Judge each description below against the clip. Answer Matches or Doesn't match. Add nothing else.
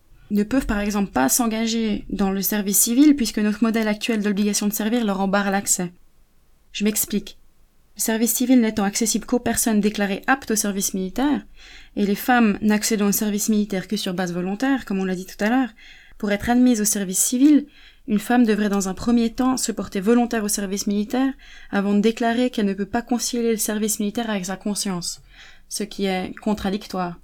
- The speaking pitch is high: Matches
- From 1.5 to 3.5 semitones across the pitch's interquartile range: Matches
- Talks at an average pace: Matches